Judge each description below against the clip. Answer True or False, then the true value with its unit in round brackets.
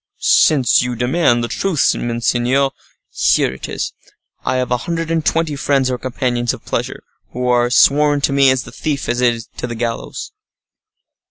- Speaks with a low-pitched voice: True (125 Hz)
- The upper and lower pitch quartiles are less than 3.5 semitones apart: True (2.8 semitones)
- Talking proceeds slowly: False (165 wpm)